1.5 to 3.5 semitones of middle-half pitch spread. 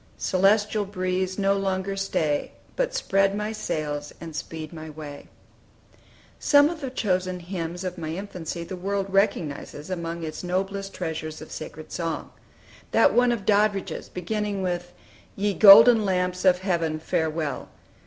Yes: average, 3.2 semitones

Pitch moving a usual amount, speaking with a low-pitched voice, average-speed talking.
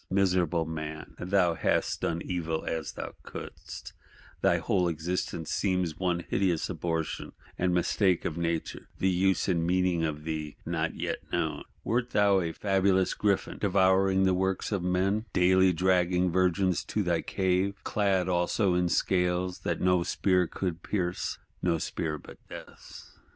No: narrow, 1.9 semitones; very low, 90 Hz; average, 145 wpm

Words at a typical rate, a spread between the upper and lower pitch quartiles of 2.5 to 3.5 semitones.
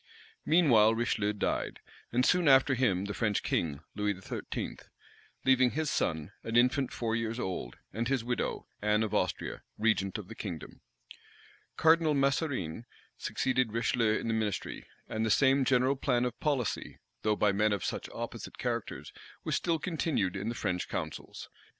No: average, 160 wpm; average, 4.3 semitones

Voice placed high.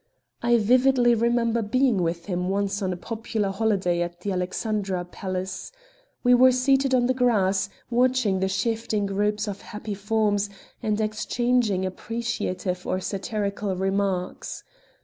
Yes: high, 210 Hz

